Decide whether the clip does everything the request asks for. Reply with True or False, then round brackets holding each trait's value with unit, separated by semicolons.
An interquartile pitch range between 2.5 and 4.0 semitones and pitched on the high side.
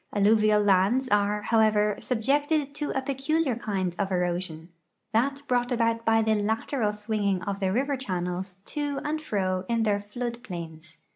False (4.6 semitones; 215 Hz)